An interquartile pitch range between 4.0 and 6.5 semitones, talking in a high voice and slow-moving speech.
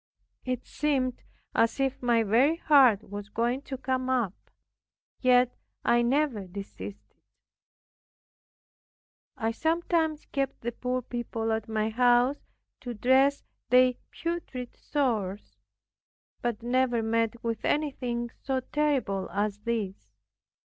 No: average, 3.1 semitones; high, 245 Hz; slow, 115 wpm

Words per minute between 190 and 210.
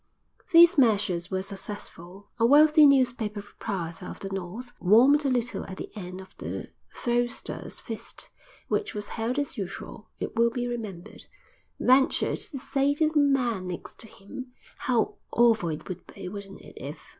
No: average, 165 wpm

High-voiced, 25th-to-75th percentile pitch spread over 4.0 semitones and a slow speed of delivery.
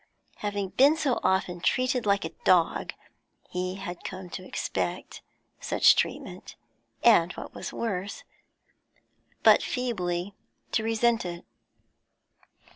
Yes: high, 195 Hz; average, 4.4 semitones; slow, 115 wpm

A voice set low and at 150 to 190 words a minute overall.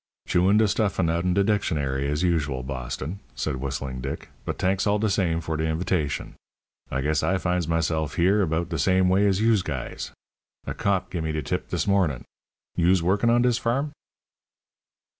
Yes: very low, 85 Hz; average, 180 wpm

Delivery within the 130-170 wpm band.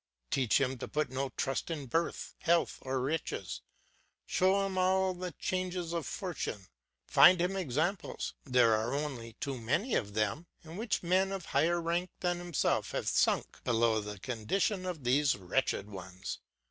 Yes: average, 160 wpm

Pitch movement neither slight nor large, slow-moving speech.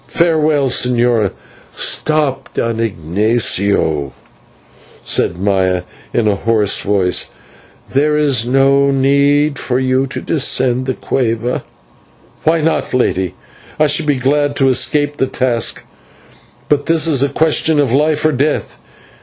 Yes: average, 4.2 semitones; slow, 130 wpm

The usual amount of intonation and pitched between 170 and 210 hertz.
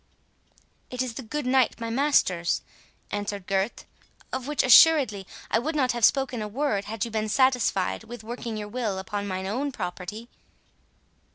No: average, 4.1 semitones; high, 225 Hz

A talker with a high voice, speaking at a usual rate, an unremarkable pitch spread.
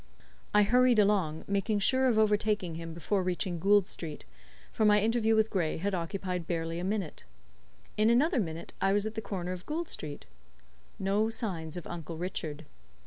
Yes: high, 195 Hz; average, 175 wpm; average, 4.2 semitones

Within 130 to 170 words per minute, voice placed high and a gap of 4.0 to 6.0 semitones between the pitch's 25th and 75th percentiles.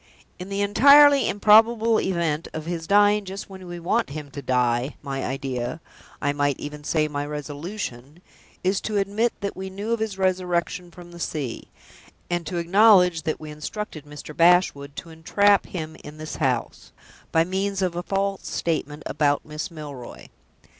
No: average, 165 wpm; medium, 170 Hz; average, 5.0 semitones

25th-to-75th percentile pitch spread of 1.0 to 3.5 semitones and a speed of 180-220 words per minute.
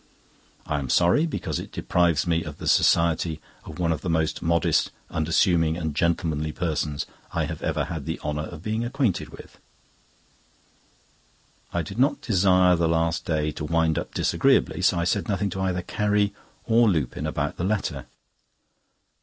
No: average, 3.2 semitones; average, 165 wpm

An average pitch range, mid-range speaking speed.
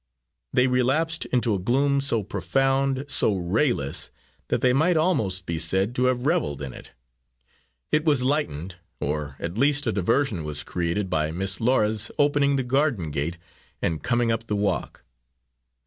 No: wide, 7.4 semitones; average, 160 wpm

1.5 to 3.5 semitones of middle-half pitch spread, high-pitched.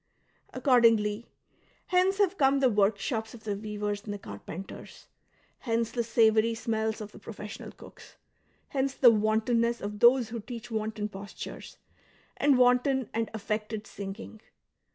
Yes: narrow, 2.6 semitones; high, 225 Hz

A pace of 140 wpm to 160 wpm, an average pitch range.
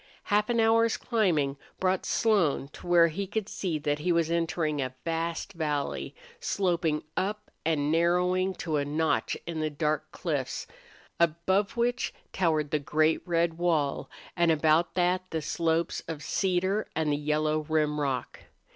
Yes: average, 155 wpm; average, 3.2 semitones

